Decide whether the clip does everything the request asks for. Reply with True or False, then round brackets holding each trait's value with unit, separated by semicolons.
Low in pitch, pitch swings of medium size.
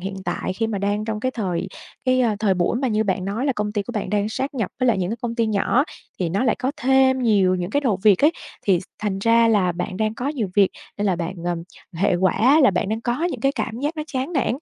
False (215 Hz; 4.7 semitones)